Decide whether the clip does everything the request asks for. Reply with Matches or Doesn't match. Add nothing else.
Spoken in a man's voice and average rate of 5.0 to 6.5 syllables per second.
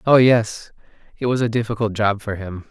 Matches